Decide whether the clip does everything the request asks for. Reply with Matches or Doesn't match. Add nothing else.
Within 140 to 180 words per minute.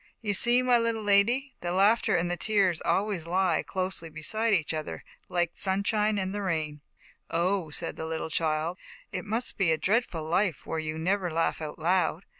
Doesn't match